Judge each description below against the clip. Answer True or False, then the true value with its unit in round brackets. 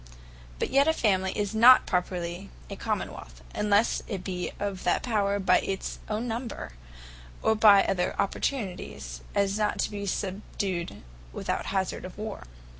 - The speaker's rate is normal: True (160 wpm)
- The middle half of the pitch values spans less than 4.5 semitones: True (2.9 semitones)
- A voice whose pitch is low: False (200 Hz)